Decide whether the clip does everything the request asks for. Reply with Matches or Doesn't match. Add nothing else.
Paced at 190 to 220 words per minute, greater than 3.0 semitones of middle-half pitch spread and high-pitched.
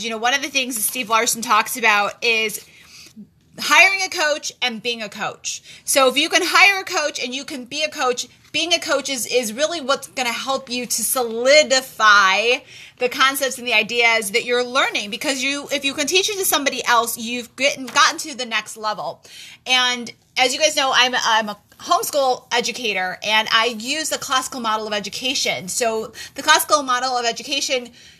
Matches